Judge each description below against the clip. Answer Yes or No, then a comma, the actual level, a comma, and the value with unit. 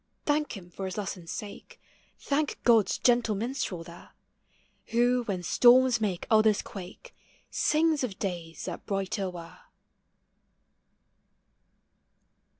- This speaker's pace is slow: Yes, slow, 110 wpm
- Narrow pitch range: No, average, 5.0 semitones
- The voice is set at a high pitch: Yes, high, 210 Hz